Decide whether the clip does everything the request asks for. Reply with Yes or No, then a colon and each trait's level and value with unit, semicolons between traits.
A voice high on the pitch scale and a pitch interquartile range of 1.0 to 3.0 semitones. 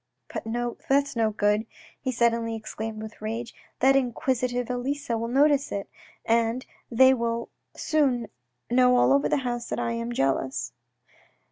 Yes: high, 235 Hz; narrow, 2.4 semitones